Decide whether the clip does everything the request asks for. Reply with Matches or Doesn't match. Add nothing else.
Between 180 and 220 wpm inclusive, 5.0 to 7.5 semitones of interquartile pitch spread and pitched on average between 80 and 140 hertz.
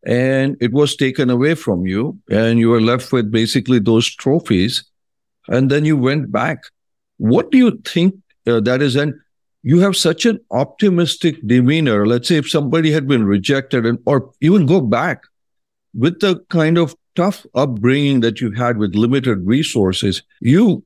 Doesn't match